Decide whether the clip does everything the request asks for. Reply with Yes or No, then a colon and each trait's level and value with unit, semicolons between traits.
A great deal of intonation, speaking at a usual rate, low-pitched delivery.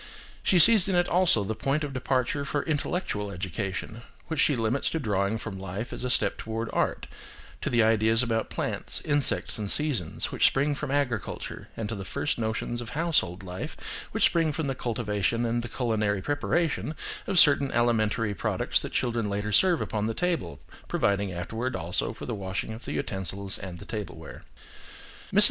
Yes: wide, 5.7 semitones; average, 180 wpm; low, 115 Hz